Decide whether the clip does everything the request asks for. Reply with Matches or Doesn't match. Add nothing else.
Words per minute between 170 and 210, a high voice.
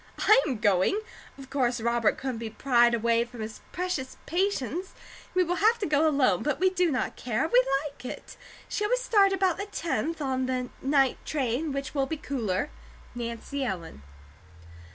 Matches